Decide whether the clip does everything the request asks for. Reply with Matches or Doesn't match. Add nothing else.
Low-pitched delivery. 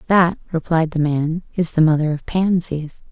Doesn't match